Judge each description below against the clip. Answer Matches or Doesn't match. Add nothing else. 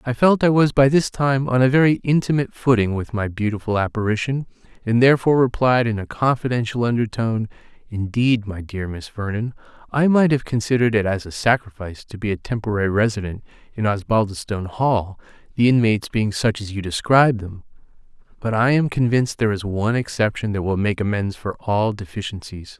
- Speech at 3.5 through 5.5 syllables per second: Doesn't match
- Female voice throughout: Doesn't match